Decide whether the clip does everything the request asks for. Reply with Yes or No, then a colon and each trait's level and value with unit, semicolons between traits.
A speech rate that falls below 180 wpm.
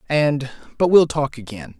Yes: slow, 135 wpm